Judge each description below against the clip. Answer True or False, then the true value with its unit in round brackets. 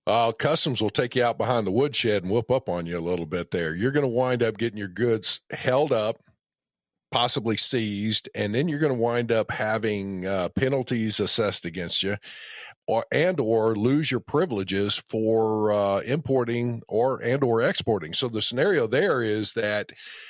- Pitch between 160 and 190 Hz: False (110 Hz)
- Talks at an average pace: True (185 wpm)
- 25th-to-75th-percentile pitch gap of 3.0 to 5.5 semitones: True (3.5 semitones)